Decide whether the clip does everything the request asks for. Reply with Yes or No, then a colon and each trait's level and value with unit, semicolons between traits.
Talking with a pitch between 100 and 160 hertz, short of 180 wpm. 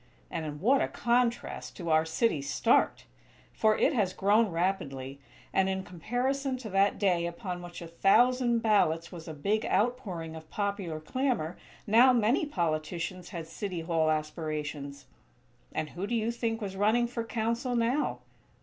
No: high, 195 Hz; average, 160 wpm